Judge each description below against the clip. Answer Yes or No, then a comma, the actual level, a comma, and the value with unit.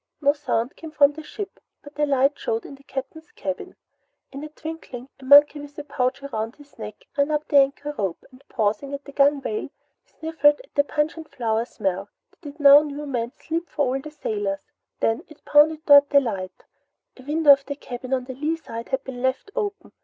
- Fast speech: Yes, fast, 210 wpm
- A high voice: Yes, very high, 280 Hz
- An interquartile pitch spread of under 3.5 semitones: Yes, average, 2.8 semitones